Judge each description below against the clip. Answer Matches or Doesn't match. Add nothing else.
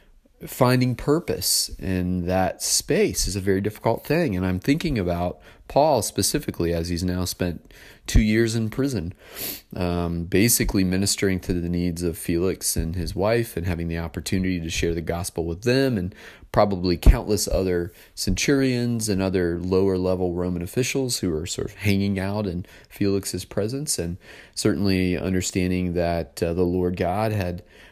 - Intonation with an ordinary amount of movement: Matches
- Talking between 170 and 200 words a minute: Doesn't match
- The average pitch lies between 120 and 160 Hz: Doesn't match